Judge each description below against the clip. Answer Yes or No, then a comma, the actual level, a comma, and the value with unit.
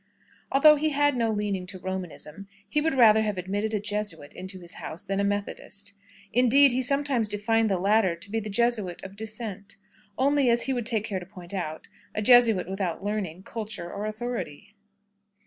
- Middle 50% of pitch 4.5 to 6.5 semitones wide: No, average, 3.8 semitones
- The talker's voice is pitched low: No, high, 210 Hz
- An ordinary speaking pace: Yes, average, 185 wpm